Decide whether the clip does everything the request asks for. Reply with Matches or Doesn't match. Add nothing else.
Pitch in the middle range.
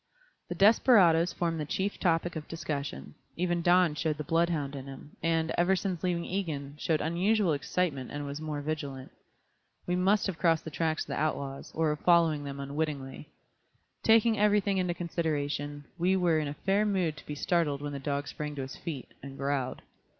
Matches